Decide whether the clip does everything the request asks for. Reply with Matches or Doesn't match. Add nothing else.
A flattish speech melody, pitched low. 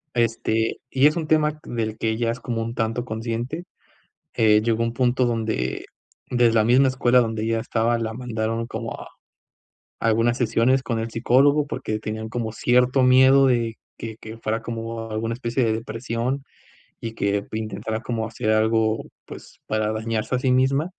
Matches